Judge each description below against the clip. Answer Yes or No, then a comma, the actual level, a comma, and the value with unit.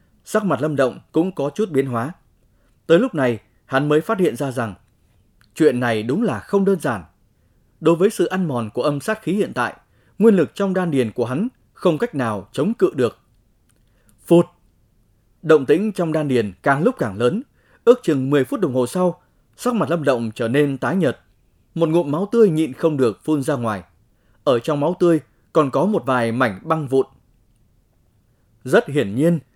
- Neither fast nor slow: Yes, average, 200 wpm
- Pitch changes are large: Yes, wide, 6.5 semitones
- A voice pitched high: No, low, 135 Hz